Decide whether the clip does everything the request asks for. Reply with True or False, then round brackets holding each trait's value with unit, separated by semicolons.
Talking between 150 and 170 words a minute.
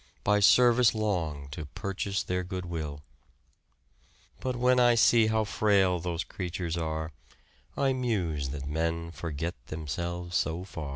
False (135 wpm)